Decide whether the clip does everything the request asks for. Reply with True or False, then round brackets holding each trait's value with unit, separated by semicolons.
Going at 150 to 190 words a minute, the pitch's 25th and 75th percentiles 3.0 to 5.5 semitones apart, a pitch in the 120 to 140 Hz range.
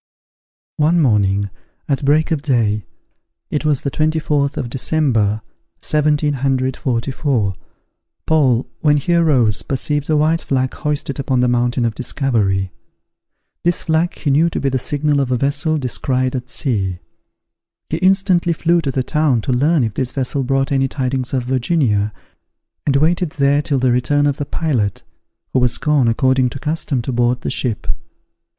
True (160 wpm; 3.5 semitones; 135 Hz)